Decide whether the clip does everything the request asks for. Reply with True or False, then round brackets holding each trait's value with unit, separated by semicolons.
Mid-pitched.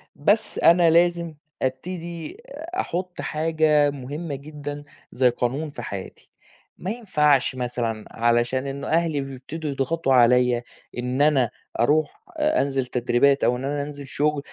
True (145 Hz)